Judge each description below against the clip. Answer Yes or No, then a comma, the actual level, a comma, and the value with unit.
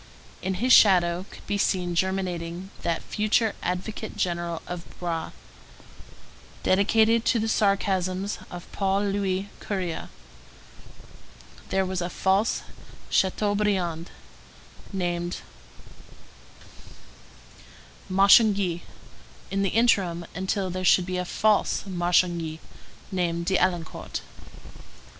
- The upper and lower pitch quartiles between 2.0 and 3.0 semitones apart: Yes, narrow, 2.4 semitones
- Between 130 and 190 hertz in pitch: Yes, medium, 185 Hz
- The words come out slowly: Yes, slow, 95 wpm